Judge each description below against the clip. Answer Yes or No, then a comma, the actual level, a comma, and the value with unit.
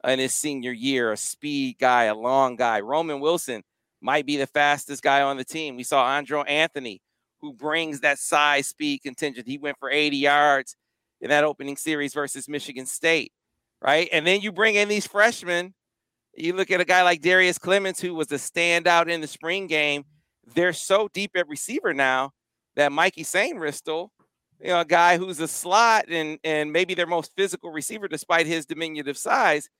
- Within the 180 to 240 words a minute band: Yes, average, 190 wpm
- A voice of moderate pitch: Yes, medium, 155 Hz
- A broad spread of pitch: No, average, 3.9 semitones